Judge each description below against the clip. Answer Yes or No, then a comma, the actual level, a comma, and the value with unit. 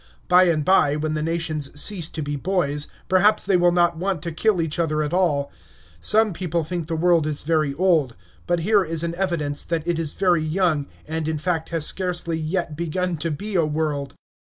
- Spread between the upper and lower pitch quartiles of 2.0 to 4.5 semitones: Yes, average, 2.7 semitones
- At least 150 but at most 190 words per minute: No, fast, 205 wpm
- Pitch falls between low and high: Yes, medium, 165 Hz